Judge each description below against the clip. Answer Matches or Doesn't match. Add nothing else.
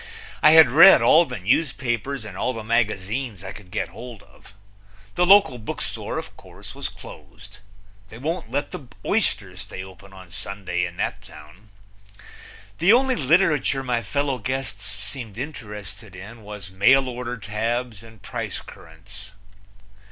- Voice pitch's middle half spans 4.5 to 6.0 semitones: Matches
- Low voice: Matches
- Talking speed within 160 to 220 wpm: Doesn't match